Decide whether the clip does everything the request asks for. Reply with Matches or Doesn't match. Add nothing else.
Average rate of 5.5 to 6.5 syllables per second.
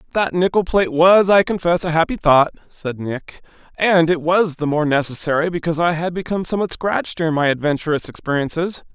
Matches